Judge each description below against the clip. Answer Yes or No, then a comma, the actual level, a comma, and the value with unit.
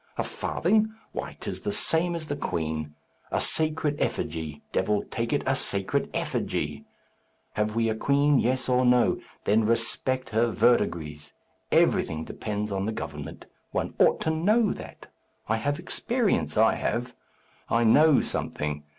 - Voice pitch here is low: Yes, low, 120 Hz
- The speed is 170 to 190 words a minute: No, average, 150 wpm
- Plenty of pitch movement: Yes, wide, 6.0 semitones